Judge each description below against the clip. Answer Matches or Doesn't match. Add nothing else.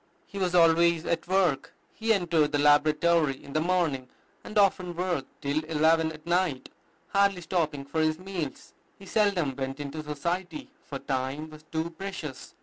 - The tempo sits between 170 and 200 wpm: Doesn't match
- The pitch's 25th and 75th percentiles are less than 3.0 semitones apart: Doesn't match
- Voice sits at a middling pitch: Matches